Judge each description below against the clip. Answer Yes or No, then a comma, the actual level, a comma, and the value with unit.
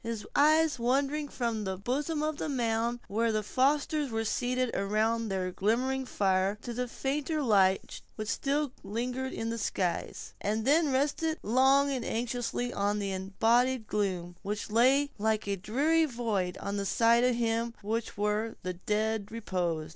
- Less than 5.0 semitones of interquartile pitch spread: Yes, average, 4.2 semitones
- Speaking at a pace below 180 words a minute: Yes, average, 160 wpm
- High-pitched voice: Yes, high, 230 Hz